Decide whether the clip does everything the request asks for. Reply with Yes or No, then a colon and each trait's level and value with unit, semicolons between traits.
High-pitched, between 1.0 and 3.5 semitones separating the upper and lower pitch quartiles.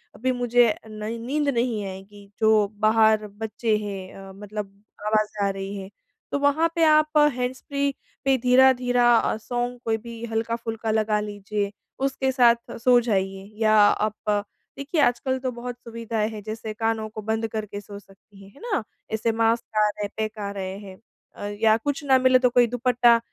Yes: high, 225 Hz; average, 2.9 semitones